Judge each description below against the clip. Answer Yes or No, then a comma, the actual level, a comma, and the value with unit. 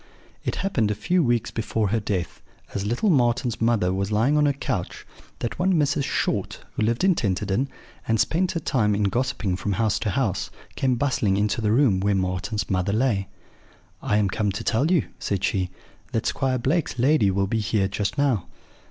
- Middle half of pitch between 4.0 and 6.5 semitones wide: Yes, average, 5.1 semitones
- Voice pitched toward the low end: Yes, low, 110 Hz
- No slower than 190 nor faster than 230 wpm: Yes, average, 195 wpm